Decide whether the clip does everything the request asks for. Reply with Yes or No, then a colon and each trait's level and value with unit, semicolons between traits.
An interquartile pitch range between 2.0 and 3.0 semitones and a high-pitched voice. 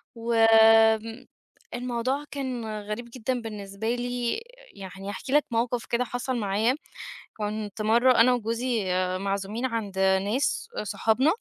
Yes: narrow, 2.6 semitones; high, 230 Hz